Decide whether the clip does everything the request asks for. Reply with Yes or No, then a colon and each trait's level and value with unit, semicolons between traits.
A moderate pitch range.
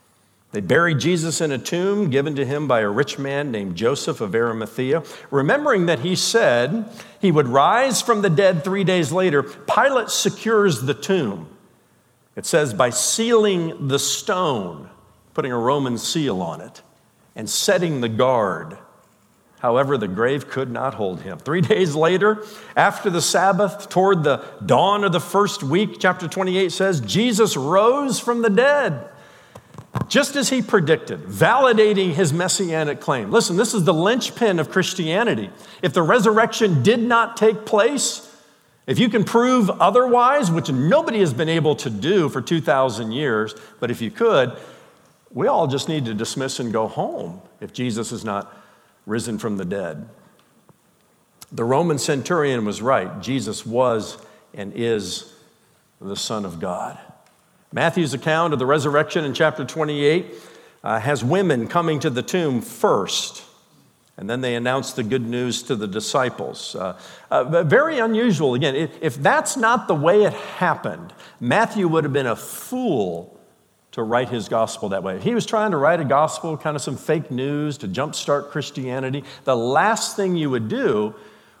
No: wide, 7.2 semitones